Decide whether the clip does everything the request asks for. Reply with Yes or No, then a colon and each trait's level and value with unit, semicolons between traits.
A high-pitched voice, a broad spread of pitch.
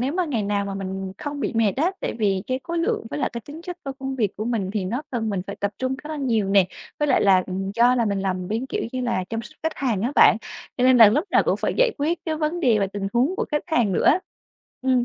Yes: high, 240 Hz; wide, 6.3 semitones